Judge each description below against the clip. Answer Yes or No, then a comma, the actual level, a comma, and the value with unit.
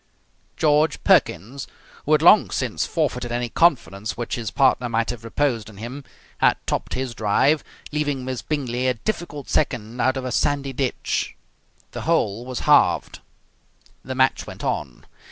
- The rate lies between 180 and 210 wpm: No, average, 155 wpm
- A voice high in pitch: No, low, 130 Hz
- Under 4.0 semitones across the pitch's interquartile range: Yes, average, 3.6 semitones